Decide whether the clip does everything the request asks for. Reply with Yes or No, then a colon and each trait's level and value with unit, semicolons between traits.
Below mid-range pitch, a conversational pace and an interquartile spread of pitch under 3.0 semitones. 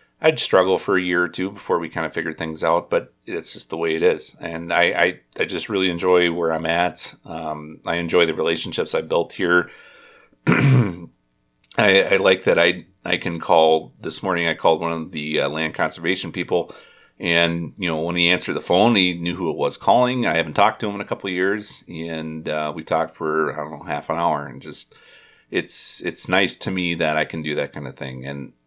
No: very low, 85 Hz; fast, 230 wpm; narrow, 2.4 semitones